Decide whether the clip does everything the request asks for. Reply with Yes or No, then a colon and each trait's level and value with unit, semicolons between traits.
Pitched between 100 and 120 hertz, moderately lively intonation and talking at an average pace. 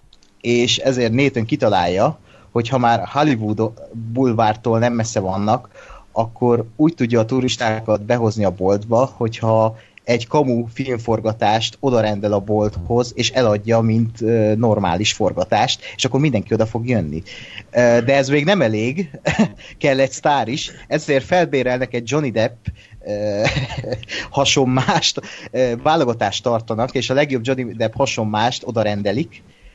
Yes: low, 115 Hz; average, 3.0 semitones; average, 135 wpm